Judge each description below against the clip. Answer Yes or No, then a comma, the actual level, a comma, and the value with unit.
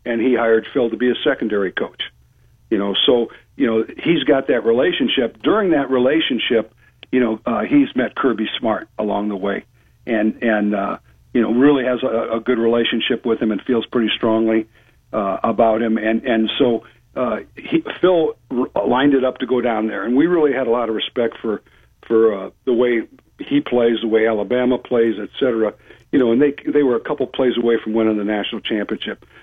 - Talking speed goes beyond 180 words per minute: Yes, fast, 205 wpm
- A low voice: Yes, low, 115 Hz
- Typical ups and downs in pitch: No, narrow, 2.2 semitones